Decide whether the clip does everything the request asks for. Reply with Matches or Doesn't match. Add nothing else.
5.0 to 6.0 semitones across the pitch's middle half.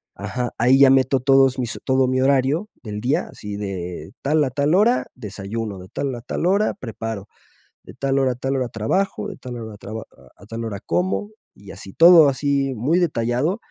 Doesn't match